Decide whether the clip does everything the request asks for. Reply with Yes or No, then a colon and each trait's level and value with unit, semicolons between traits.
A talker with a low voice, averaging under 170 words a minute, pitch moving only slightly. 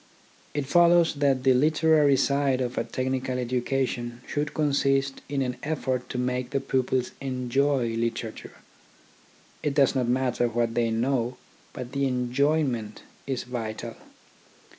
Yes: low, 130 Hz; slow, 135 wpm; narrow, 2.3 semitones